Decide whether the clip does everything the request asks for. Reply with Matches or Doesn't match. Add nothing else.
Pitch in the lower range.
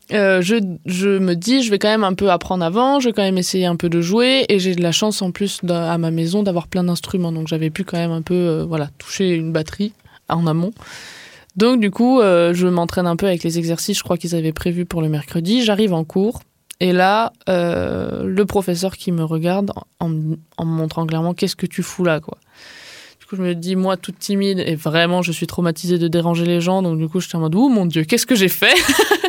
Doesn't match